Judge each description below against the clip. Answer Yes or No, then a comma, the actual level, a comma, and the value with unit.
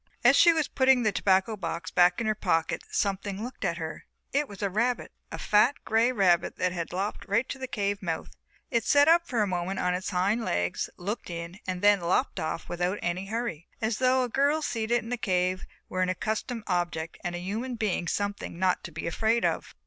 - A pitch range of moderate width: Yes, average, 4.7 semitones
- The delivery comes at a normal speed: No, fast, 220 wpm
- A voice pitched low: No, high, 200 Hz